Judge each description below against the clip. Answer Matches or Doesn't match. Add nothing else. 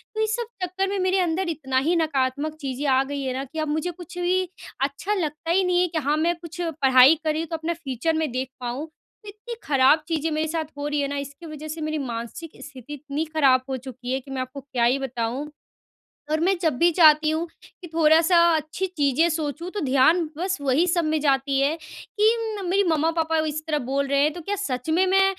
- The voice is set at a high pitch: Matches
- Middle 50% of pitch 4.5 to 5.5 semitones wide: Doesn't match